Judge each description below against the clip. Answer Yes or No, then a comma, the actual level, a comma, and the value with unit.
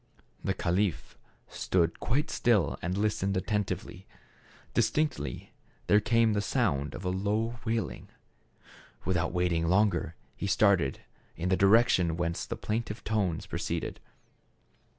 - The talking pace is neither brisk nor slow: No, slow, 130 wpm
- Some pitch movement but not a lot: Yes, average, 4.1 semitones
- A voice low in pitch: Yes, low, 100 Hz